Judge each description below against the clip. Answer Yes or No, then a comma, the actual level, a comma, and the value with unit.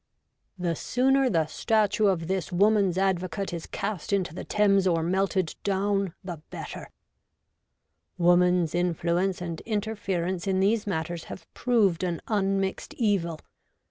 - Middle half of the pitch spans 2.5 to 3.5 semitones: Yes, average, 2.8 semitones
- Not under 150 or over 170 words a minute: No, average, 140 wpm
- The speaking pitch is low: No, high, 190 Hz